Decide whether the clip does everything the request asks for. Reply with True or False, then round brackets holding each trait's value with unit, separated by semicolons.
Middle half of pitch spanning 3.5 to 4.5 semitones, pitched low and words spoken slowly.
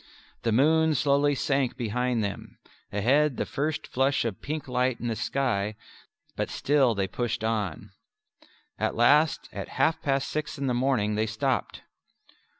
False (4.0 semitones; 130 Hz; 150 wpm)